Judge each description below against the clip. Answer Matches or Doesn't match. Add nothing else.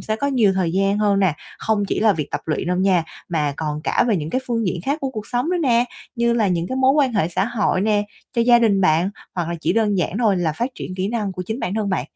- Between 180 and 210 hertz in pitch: Matches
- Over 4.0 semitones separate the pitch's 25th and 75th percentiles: Matches